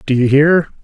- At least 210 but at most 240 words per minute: Yes, fast, 215 wpm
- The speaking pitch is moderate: Yes, medium, 145 Hz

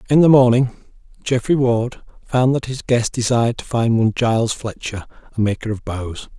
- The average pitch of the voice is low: Yes, low, 120 Hz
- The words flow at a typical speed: Yes, average, 180 wpm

